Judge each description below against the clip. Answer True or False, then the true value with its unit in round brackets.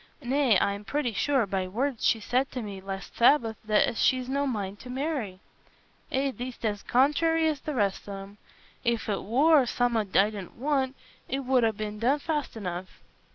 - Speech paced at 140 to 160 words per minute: False (180 wpm)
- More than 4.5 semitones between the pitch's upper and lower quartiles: True (4.9 semitones)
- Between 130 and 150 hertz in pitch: False (240 Hz)